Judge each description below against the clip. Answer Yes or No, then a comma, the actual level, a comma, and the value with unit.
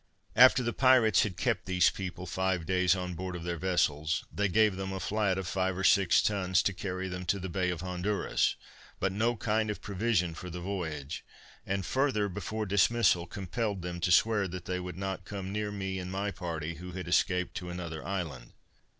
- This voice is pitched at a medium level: No, very low, 95 Hz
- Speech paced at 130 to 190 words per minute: No, average, 200 wpm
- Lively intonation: No, narrow, 2.4 semitones